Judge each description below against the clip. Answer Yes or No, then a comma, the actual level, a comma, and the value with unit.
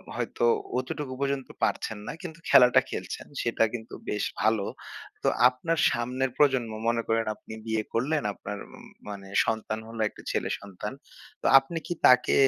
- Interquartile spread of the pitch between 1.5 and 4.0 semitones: Yes, average, 3.2 semitones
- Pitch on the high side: No, low, 120 Hz